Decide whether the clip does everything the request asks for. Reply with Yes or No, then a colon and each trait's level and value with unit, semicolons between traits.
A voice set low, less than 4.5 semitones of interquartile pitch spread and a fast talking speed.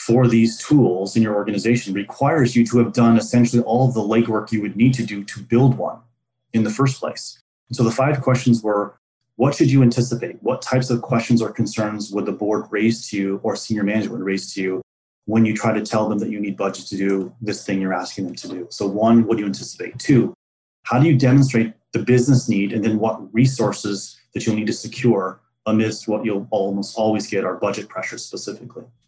Yes: low, 110 Hz; average, 2.7 semitones; fast, 225 wpm